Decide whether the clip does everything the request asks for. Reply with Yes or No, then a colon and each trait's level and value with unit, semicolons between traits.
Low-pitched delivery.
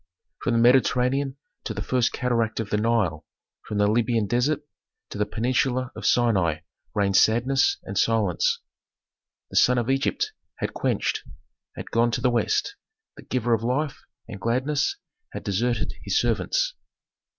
Yes: low, 120 Hz